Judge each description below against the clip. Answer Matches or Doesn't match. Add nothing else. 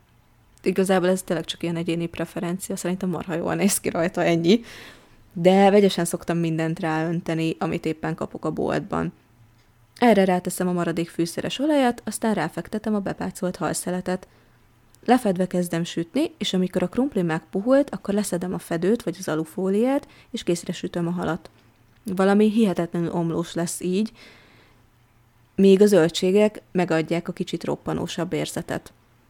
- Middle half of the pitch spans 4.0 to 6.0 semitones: Doesn't match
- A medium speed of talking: Matches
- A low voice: Doesn't match